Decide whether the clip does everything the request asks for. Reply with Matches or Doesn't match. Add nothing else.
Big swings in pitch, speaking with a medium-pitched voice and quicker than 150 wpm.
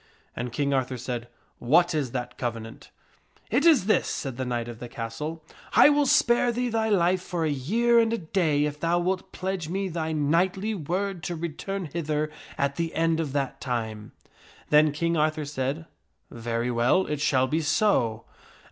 Matches